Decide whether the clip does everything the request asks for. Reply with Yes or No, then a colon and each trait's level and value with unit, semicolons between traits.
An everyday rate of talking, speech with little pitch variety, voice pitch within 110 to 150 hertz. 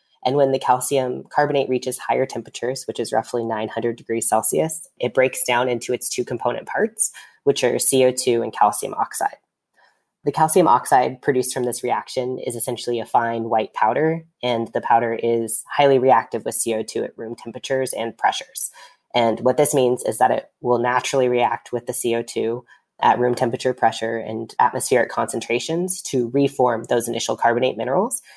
Yes: average, 170 wpm; narrow, 2.1 semitones; low, 125 Hz